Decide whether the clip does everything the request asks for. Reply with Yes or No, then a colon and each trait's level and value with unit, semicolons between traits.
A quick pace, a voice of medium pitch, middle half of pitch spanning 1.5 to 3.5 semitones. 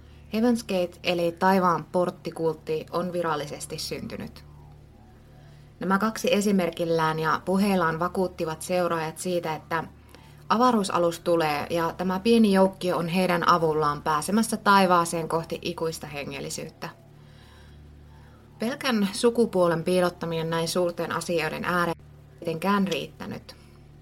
No: average, 100 wpm; medium, 175 Hz; narrow, 2.5 semitones